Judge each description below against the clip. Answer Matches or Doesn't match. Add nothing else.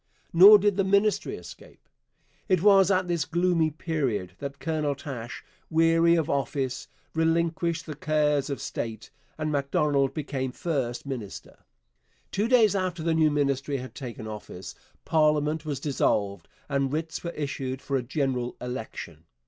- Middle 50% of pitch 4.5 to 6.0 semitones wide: Doesn't match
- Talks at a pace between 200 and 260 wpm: Doesn't match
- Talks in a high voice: Doesn't match